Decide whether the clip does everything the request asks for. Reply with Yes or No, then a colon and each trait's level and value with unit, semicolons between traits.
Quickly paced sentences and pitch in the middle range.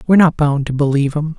Yes: fast, 260 wpm; medium, 150 Hz